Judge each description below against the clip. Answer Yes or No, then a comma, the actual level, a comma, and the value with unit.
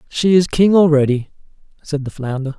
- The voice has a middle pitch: Yes, medium, 150 Hz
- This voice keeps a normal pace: Yes, average, 160 wpm